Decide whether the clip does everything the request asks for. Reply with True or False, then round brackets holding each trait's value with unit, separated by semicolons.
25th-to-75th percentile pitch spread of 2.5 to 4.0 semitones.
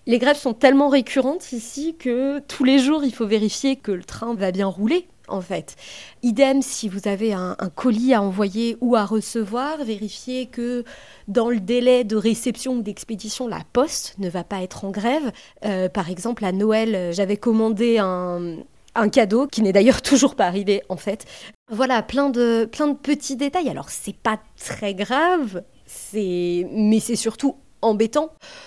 False (4.4 semitones)